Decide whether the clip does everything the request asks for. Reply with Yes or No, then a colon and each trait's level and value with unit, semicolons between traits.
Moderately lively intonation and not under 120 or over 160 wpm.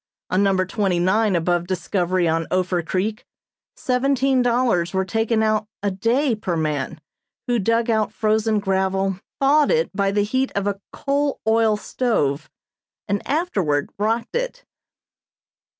Yes: average, 4.3 semitones; average, 140 wpm